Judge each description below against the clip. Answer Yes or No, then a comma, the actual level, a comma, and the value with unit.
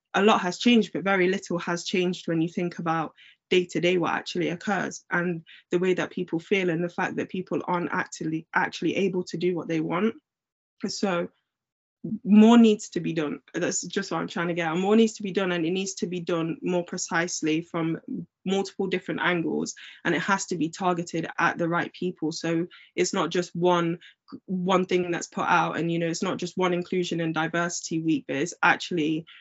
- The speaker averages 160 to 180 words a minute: No, fast, 205 wpm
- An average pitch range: No, narrow, 2.2 semitones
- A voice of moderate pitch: Yes, medium, 180 Hz